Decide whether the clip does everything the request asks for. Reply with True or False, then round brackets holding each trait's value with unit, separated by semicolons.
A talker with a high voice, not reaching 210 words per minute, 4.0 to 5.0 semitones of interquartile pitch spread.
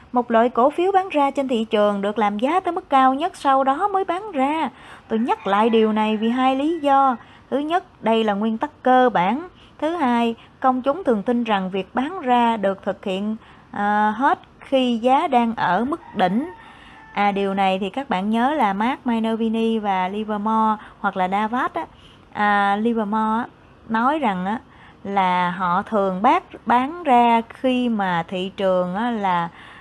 True (230 Hz; 175 wpm; 4.6 semitones)